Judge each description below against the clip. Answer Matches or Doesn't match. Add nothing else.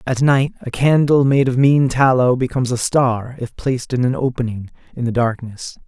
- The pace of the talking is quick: Doesn't match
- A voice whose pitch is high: Doesn't match